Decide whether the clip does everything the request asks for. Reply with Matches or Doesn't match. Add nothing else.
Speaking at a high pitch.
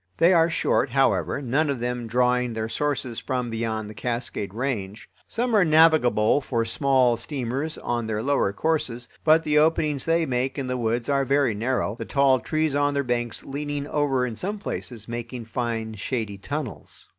Doesn't match